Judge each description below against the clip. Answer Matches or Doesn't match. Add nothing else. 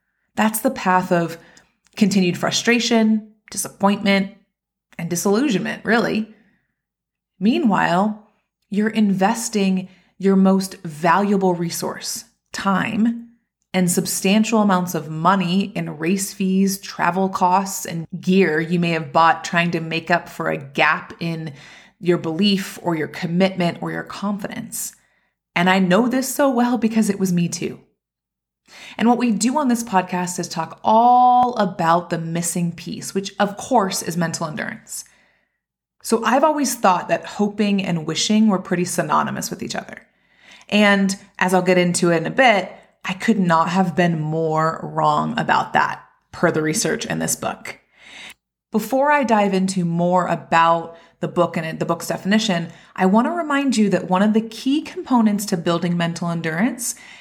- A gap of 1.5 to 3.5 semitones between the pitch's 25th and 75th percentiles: Doesn't match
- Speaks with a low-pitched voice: Doesn't match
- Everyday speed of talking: Matches